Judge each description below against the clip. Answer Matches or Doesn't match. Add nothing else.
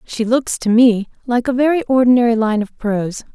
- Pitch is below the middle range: Doesn't match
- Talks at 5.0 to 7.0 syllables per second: Matches